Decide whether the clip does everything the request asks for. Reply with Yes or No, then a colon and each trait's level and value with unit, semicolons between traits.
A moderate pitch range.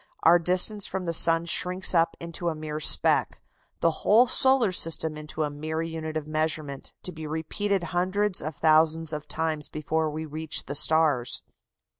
No: narrow, 2.1 semitones